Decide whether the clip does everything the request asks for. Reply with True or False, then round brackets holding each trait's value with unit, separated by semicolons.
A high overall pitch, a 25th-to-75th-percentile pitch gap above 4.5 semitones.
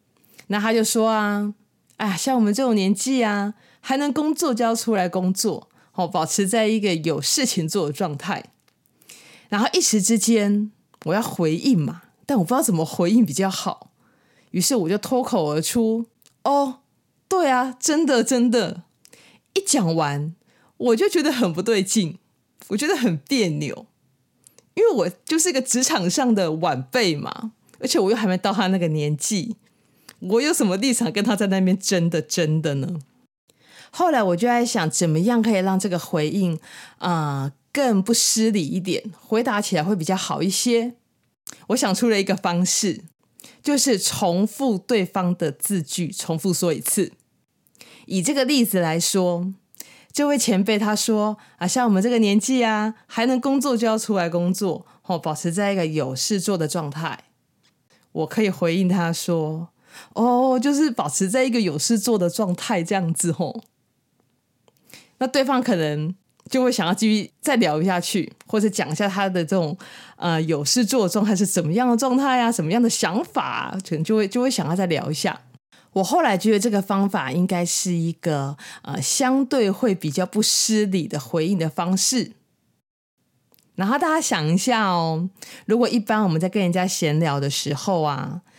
True (200 Hz; 5.1 semitones)